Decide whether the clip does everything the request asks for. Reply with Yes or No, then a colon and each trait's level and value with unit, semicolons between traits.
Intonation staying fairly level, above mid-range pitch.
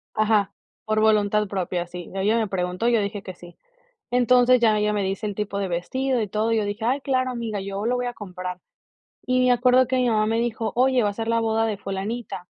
No: average, 3.3 semitones; high, 215 Hz